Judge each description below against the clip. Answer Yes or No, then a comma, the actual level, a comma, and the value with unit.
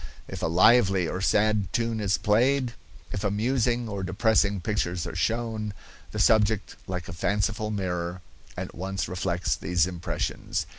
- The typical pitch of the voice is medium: No, low, 100 Hz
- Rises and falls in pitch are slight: No, average, 3.3 semitones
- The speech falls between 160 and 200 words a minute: No, average, 145 wpm